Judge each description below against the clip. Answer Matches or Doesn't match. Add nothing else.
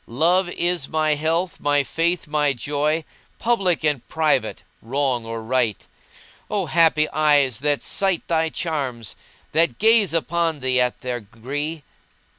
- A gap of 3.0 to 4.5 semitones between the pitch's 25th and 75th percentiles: Matches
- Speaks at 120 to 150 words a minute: Matches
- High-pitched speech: Doesn't match